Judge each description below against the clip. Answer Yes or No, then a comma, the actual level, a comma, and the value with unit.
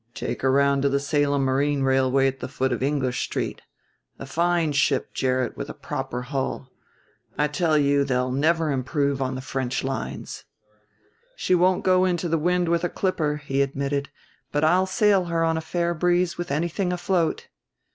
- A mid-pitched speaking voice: Yes, medium, 145 Hz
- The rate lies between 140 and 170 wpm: No, average, 180 wpm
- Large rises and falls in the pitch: No, average, 4.2 semitones